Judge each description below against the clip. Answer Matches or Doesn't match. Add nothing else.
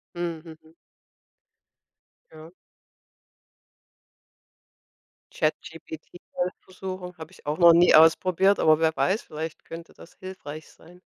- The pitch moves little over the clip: Matches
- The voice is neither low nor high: Matches